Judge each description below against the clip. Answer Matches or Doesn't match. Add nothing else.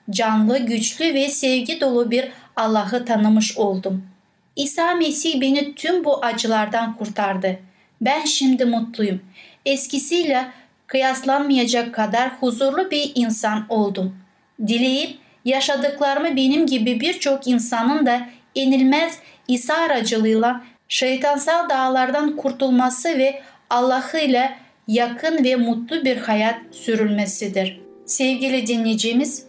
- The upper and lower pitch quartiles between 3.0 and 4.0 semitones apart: Matches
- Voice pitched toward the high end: Matches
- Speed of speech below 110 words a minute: Matches